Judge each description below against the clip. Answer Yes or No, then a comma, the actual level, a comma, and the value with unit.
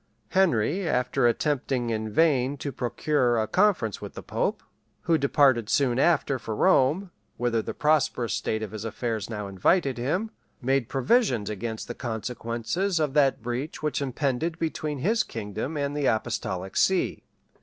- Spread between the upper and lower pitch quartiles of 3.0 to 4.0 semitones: No, average, 4.9 semitones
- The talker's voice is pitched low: Yes, low, 130 Hz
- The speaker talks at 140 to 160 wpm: Yes, average, 155 wpm